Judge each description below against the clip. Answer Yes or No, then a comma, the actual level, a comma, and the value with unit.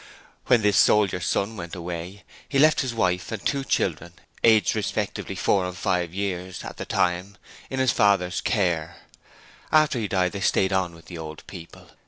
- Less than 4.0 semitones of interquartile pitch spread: Yes, average, 3.2 semitones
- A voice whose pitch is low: Yes, very low, 95 Hz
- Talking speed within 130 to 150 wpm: No, average, 180 wpm